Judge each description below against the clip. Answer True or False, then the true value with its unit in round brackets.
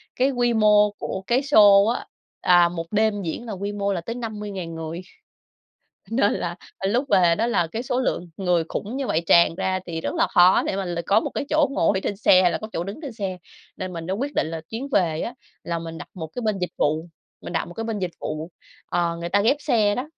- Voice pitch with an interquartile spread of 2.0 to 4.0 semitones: False (4.6 semitones)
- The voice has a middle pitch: False (195 Hz)